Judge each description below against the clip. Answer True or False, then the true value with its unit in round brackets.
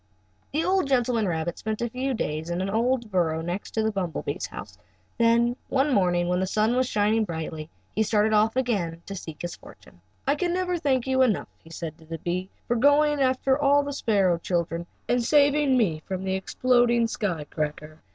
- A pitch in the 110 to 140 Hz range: False (220 Hz)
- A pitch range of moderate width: False (6.9 semitones)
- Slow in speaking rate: False (200 wpm)